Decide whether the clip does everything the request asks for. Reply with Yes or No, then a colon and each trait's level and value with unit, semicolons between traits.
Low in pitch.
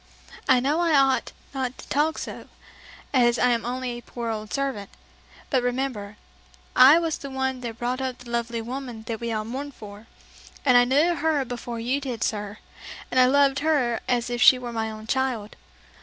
No: very high, 250 Hz